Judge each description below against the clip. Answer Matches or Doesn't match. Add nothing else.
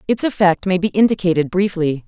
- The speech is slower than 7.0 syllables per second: Matches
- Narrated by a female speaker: Matches